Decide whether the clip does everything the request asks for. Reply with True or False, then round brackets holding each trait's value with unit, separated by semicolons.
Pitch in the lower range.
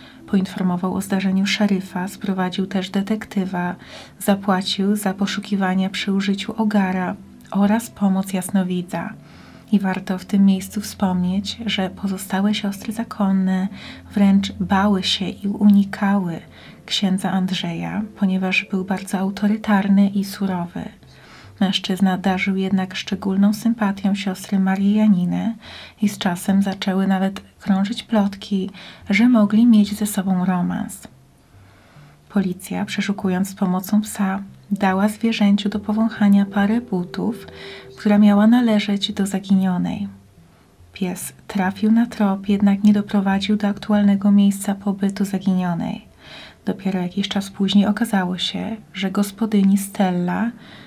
False (200 Hz)